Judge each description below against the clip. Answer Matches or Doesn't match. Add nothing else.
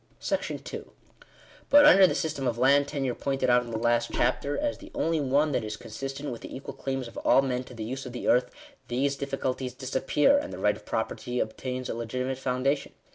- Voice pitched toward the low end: Matches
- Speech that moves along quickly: Matches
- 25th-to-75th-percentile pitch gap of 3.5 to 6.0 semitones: Doesn't match